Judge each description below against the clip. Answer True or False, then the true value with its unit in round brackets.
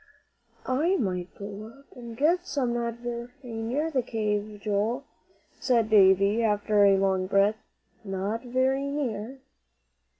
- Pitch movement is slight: False (4.0 semitones)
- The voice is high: True (225 Hz)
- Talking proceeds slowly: True (130 wpm)